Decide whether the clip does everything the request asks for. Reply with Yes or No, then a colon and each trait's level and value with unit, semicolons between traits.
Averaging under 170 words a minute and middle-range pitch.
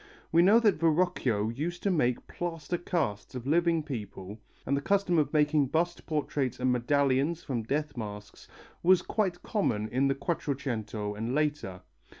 Yes: average, 155 wpm; medium, 145 Hz